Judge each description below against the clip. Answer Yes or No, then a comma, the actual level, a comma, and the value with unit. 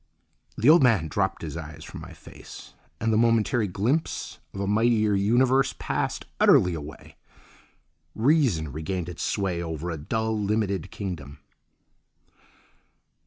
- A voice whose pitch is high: No, low, 100 Hz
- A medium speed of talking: No, slow, 130 wpm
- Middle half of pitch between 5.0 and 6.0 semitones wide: Yes, wide, 5.5 semitones